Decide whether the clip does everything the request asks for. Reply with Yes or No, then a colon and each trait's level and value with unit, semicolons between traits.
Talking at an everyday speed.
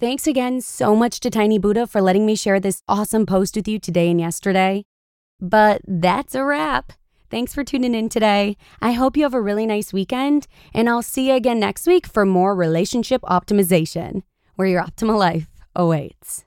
Yes: average, 190 wpm